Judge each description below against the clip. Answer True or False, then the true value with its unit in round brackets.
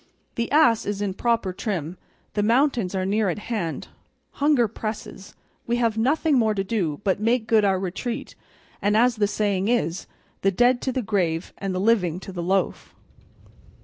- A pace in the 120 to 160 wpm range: False (180 wpm)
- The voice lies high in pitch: True (210 Hz)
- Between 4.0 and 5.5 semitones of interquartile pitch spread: False (3.6 semitones)